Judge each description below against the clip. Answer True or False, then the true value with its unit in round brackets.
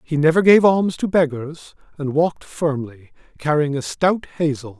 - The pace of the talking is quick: False (165 wpm)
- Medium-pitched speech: True (155 Hz)